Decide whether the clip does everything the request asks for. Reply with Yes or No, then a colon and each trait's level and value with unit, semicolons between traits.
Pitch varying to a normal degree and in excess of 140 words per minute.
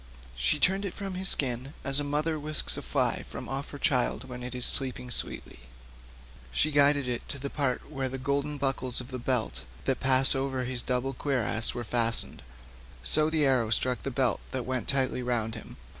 No: narrow, 2.3 semitones; average, 200 wpm